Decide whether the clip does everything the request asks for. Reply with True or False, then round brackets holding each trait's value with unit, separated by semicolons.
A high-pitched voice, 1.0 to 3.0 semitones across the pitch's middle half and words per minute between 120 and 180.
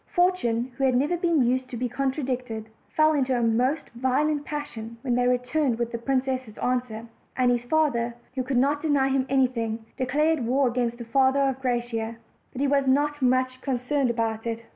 False (255 Hz; 2.6 semitones; 190 wpm)